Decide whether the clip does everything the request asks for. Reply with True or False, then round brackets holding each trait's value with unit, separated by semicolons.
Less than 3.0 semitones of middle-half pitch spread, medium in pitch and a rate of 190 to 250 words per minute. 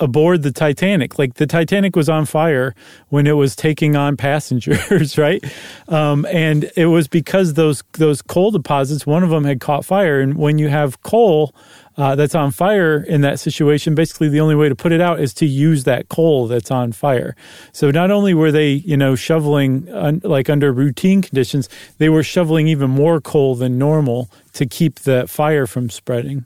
True (2.5 semitones; 150 Hz; 195 wpm)